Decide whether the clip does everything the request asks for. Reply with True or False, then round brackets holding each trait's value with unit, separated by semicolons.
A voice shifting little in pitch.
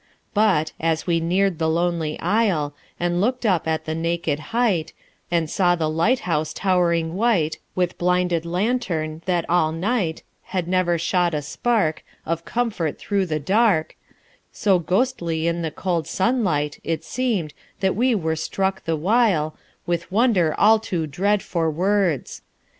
False (3.6 semitones)